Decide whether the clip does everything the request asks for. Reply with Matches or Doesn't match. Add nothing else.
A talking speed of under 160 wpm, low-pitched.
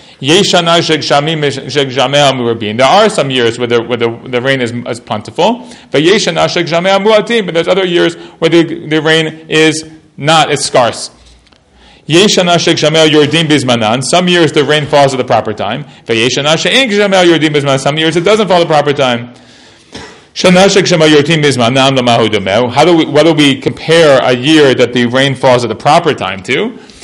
Doesn't match